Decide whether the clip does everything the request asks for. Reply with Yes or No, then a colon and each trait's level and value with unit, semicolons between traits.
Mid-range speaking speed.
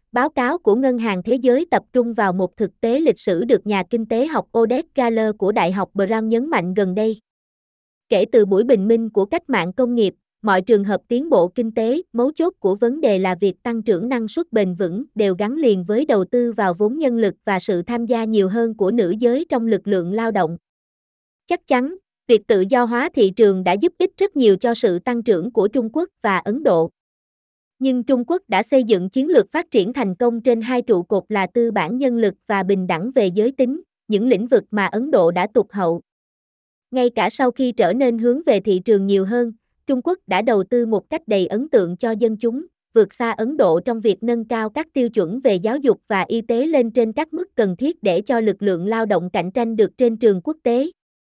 Yes: average, 240 wpm